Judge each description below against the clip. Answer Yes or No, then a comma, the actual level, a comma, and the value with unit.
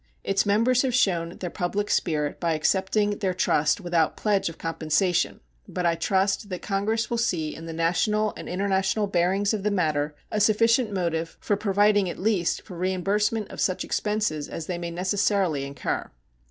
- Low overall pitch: No, high, 190 Hz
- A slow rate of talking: No, average, 175 wpm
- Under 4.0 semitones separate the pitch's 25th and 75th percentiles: Yes, average, 3.6 semitones